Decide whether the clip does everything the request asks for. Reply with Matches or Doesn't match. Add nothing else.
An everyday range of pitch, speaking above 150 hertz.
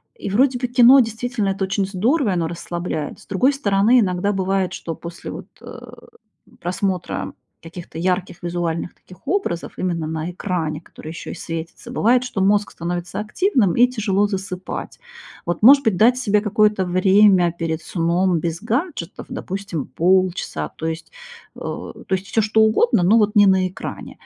Matches